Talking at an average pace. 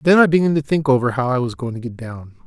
No: fast, 315 wpm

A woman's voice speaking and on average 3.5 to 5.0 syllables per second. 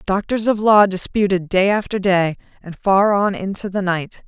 Yes: female; 4.6 syllables/s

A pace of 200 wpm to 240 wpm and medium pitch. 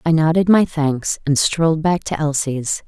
No: average, 190 wpm; medium, 155 Hz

